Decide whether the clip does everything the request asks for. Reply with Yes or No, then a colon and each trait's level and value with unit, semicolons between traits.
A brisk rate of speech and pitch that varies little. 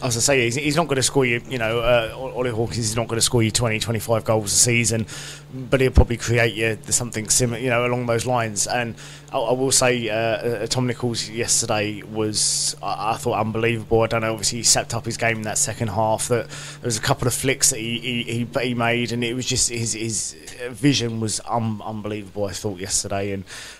Yes: fast, 215 wpm; narrow, 2.1 semitones